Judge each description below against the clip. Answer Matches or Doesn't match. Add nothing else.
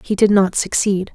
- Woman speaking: Matches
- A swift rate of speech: Matches